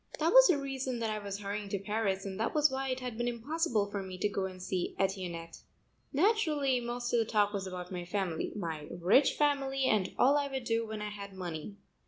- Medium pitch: No, high, 215 Hz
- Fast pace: Yes, fast, 230 wpm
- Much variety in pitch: Yes, wide, 5.7 semitones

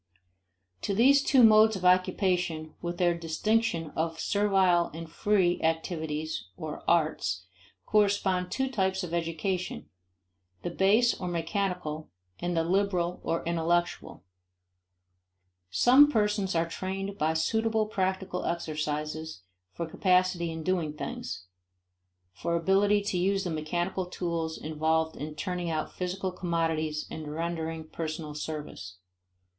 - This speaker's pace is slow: Yes, slow, 120 wpm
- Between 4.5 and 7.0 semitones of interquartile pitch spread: No, average, 3.1 semitones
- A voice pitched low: No, medium, 175 Hz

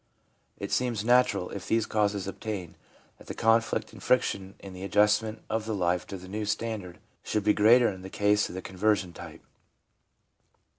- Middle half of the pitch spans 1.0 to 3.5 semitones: Yes, average, 2.7 semitones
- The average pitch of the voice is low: Yes, low, 105 Hz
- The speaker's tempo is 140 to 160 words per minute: No, average, 170 wpm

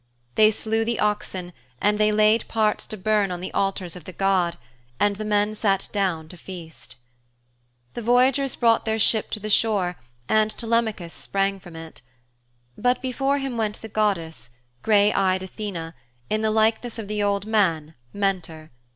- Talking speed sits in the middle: Yes, average, 170 wpm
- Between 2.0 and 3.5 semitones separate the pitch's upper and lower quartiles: Yes, average, 2.9 semitones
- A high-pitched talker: Yes, high, 210 Hz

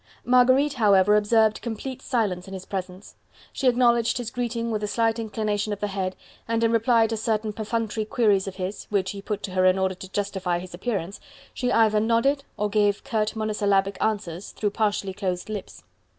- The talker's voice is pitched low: No, high, 210 Hz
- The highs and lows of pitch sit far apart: No, average, 2.7 semitones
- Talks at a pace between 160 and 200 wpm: Yes, average, 190 wpm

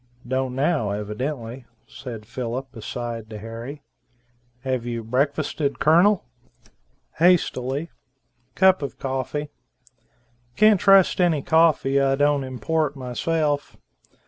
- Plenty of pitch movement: No, average, 4.2 semitones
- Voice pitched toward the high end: No, low, 135 Hz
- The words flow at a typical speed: No, slow, 100 wpm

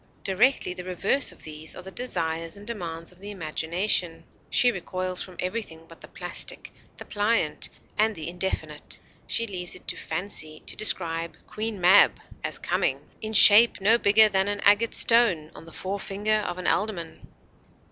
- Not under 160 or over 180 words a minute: Yes, average, 165 wpm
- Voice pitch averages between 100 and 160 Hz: No, high, 190 Hz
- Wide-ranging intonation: No, average, 4.1 semitones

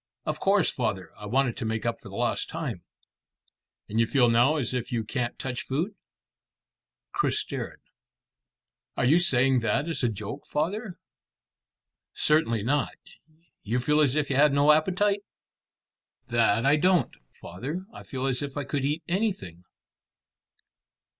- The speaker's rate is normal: Yes, average, 150 wpm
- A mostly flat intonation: No, average, 4.7 semitones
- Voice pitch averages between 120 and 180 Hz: Yes, low, 135 Hz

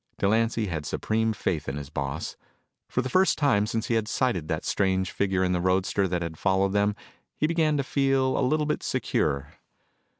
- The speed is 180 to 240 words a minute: Yes, average, 195 wpm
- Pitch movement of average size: No, wide, 6.0 semitones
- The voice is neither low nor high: No, low, 100 Hz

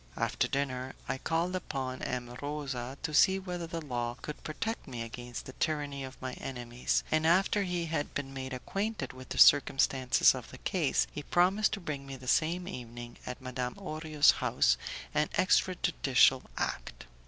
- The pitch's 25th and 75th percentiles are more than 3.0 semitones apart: Yes, average, 4.6 semitones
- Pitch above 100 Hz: Yes, medium, 140 Hz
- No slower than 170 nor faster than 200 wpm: Yes, average, 175 wpm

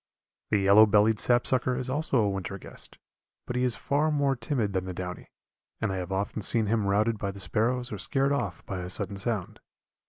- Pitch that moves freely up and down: No, average, 4.2 semitones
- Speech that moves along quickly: Yes, fast, 210 wpm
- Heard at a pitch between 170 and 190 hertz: No, low, 110 Hz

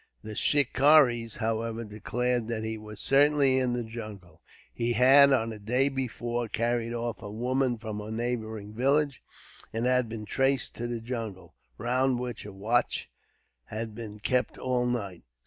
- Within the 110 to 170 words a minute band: Yes, average, 160 wpm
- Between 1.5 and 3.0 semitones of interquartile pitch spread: Yes, narrow, 2.5 semitones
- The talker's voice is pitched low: Yes, low, 120 Hz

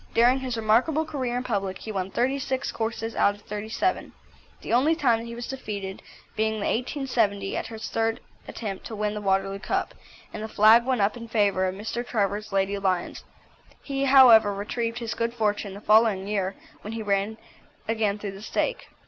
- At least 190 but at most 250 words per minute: Yes, average, 195 wpm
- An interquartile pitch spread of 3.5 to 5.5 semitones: No, average, 2.9 semitones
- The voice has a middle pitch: No, high, 220 Hz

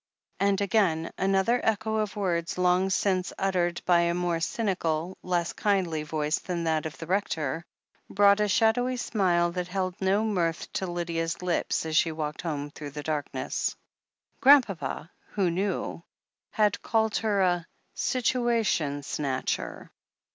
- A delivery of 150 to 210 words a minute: No, average, 140 wpm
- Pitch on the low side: No, medium, 180 Hz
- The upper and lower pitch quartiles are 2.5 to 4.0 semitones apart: Yes, average, 3.6 semitones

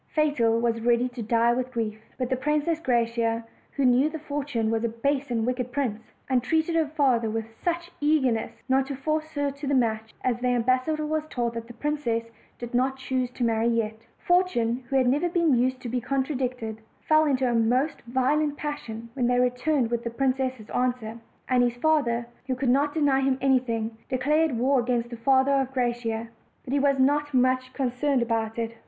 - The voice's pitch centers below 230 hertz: No, very high, 255 Hz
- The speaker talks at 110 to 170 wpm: No, average, 200 wpm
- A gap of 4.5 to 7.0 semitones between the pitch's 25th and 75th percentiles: No, average, 3.2 semitones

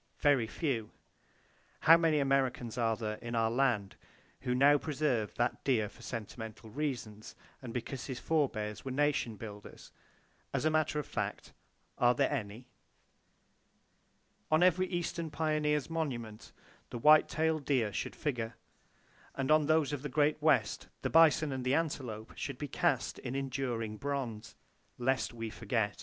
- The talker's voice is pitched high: No, low, 135 Hz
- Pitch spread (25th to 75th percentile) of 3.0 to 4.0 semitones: No, average, 4.7 semitones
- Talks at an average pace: Yes, average, 150 wpm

